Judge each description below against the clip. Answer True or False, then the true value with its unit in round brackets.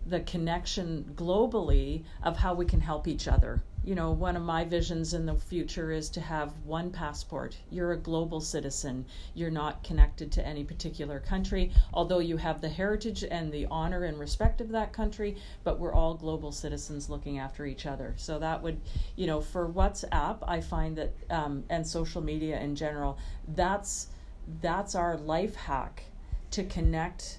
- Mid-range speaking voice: True (165 Hz)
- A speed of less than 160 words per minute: False (175 wpm)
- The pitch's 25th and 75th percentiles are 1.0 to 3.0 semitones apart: True (2.6 semitones)